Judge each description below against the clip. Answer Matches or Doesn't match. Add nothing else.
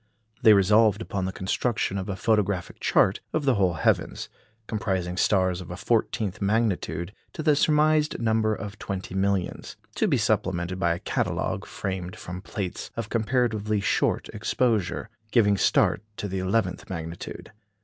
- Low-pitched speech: Matches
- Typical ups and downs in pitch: Matches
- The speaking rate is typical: Matches